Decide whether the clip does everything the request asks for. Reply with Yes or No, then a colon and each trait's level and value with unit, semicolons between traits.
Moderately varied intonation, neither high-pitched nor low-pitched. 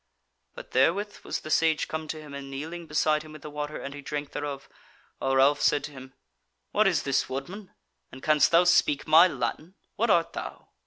Yes: average, 3.1 semitones; medium, 150 Hz